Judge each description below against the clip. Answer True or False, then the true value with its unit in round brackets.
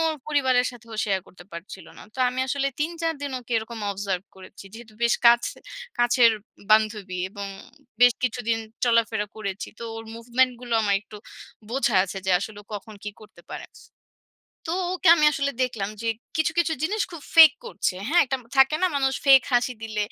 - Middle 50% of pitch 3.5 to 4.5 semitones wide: True (4.2 semitones)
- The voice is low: False (235 Hz)